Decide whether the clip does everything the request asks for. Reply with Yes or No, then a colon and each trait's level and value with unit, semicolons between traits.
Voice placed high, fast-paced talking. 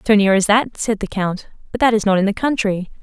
Yes: high, 210 Hz; fast, 280 wpm